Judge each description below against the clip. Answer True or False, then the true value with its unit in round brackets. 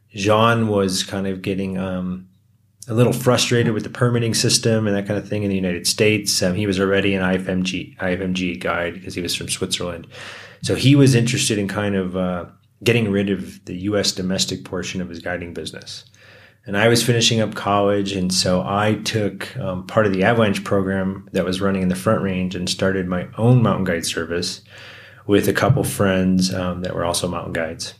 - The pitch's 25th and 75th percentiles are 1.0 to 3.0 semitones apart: True (2.7 semitones)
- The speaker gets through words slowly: False (200 wpm)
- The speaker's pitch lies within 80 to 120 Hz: True (100 Hz)